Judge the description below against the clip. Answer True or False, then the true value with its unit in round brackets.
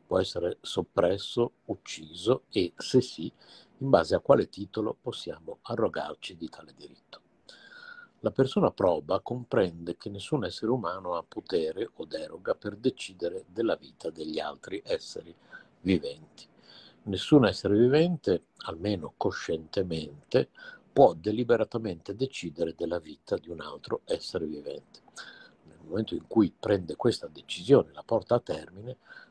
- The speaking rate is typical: True (125 wpm)